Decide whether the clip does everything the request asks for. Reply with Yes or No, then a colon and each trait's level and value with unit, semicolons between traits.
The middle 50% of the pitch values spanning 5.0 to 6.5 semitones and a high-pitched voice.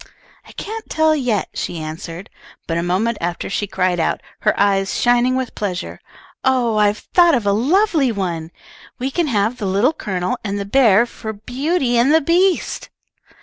Yes: wide, 5.5 semitones; high, 220 Hz